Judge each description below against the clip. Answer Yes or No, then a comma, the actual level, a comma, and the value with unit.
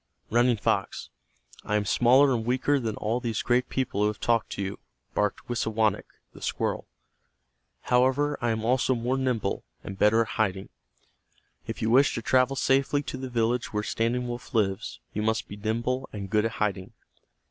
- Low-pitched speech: Yes, low, 115 Hz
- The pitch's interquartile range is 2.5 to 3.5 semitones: Yes, average, 3.1 semitones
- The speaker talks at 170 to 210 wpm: Yes, average, 180 wpm